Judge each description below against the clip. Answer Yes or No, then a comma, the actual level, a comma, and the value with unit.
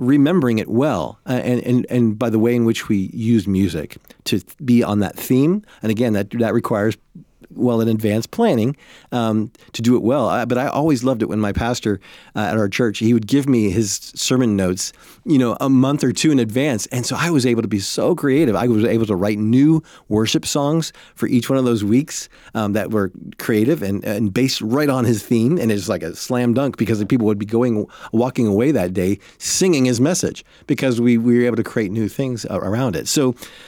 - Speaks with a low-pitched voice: Yes, low, 120 Hz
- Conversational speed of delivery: No, fast, 230 wpm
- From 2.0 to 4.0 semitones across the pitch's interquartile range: Yes, average, 3.1 semitones